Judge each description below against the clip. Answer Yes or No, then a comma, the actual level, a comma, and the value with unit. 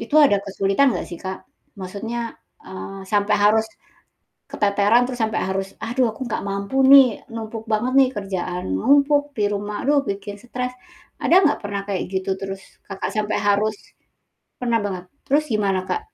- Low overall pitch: No, high, 210 Hz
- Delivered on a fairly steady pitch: No, average, 3.5 semitones